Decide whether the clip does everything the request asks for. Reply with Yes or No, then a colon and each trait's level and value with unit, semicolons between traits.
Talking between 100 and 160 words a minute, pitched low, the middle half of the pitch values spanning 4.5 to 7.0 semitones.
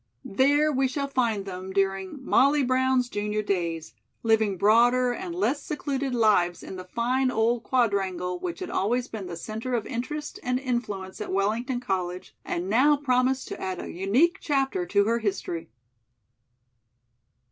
No: average, 155 wpm; high, 235 Hz; average, 5.2 semitones